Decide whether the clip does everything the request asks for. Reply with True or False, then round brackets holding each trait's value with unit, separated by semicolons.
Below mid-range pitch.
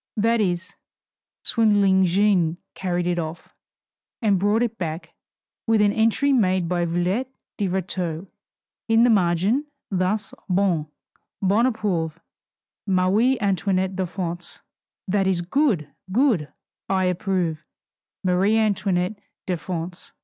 False (190 Hz)